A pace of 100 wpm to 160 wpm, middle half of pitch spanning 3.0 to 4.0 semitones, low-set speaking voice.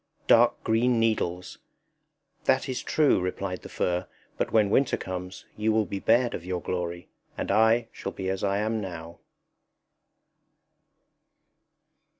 Yes: average, 140 wpm; average, 3.6 semitones; low, 100 Hz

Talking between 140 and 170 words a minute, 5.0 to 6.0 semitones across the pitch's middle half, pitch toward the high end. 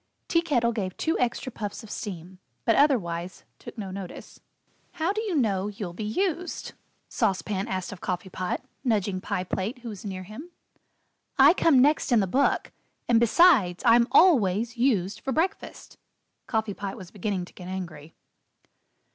Yes: average, 165 wpm; wide, 5.5 semitones; high, 210 Hz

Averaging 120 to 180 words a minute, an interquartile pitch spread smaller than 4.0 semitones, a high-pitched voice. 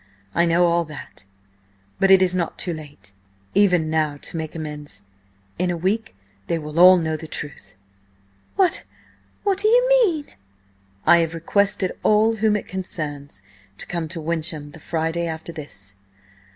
No: average, 155 wpm; average, 3.5 semitones; medium, 170 Hz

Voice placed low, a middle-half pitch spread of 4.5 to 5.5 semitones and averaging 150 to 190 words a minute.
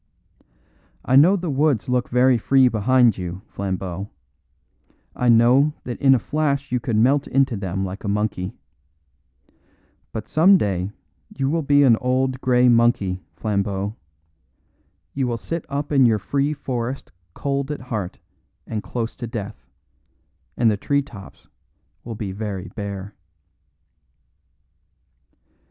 No: low, 120 Hz; average, 4.9 semitones; slow, 135 wpm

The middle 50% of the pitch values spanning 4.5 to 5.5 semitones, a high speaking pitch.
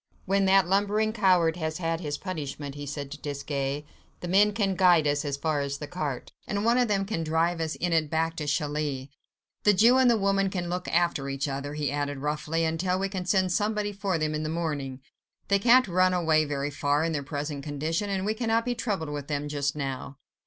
No: average, 5.0 semitones; medium, 160 Hz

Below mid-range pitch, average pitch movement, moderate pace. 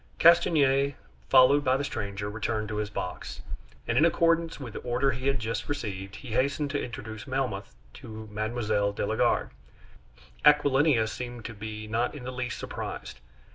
Yes: low, 120 Hz; average, 4.4 semitones; average, 170 wpm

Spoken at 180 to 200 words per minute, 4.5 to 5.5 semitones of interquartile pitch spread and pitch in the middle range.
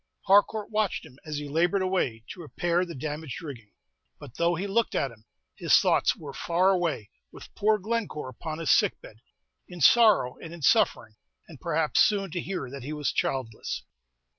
Yes: average, 185 wpm; average, 5.2 semitones; medium, 165 Hz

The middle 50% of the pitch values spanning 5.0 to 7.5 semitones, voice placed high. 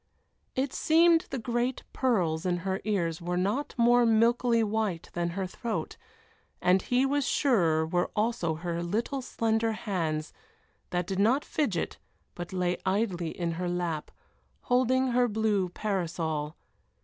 Yes: wide, 5.6 semitones; high, 200 Hz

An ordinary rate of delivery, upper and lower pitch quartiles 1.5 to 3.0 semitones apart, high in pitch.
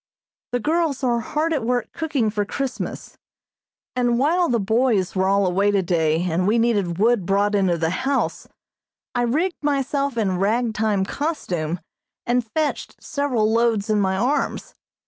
No: average, 155 wpm; wide, 5.5 semitones; high, 230 Hz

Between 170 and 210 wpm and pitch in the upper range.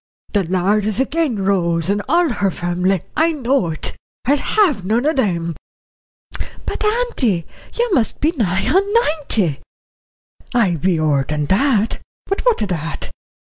No: average, 145 wpm; high, 210 Hz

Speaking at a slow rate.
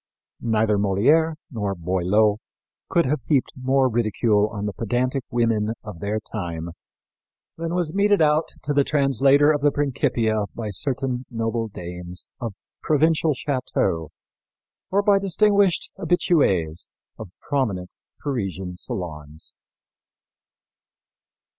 Yes: slow, 115 wpm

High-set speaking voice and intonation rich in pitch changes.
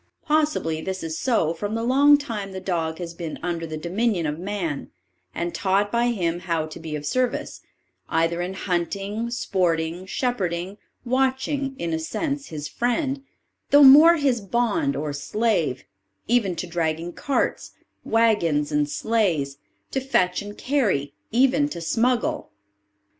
Yes: high, 195 Hz; wide, 7.0 semitones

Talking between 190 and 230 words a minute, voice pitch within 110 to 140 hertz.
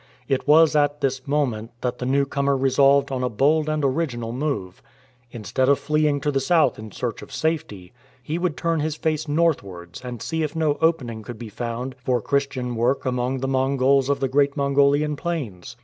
Yes: average, 195 wpm; low, 135 Hz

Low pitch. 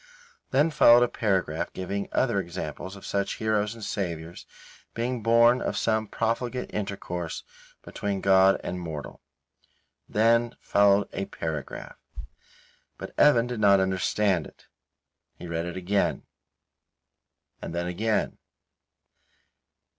Yes: low, 100 Hz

